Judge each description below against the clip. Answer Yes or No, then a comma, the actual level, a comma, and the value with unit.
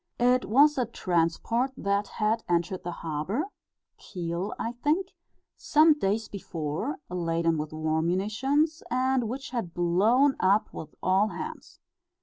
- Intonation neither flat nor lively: No, wide, 6.9 semitones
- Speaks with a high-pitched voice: Yes, high, 205 Hz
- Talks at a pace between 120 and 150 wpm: Yes, slow, 135 wpm